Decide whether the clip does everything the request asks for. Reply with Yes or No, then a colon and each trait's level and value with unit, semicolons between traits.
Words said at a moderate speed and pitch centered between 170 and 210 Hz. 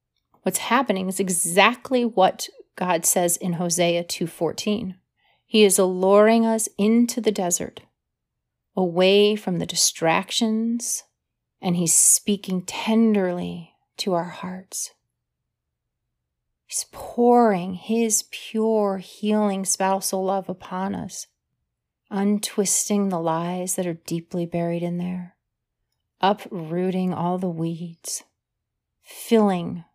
No: slow, 100 wpm; high, 190 Hz